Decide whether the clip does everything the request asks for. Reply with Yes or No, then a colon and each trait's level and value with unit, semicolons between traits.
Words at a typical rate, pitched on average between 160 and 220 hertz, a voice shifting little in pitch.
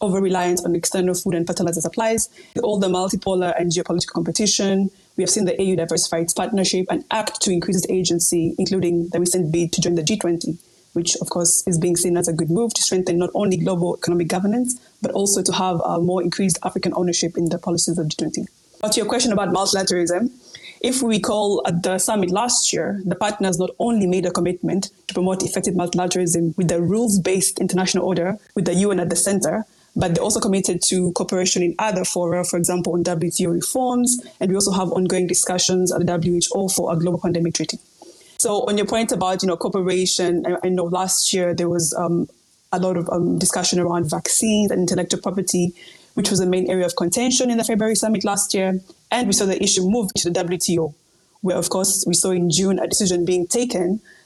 No: fast, 210 wpm; medium, 185 Hz; narrow, 2.0 semitones